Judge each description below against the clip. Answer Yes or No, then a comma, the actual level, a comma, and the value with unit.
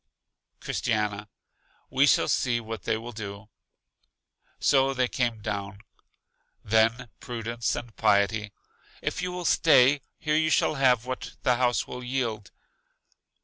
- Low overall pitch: Yes, low, 120 Hz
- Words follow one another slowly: Yes, slow, 130 wpm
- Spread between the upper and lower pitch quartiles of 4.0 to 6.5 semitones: No, average, 3.2 semitones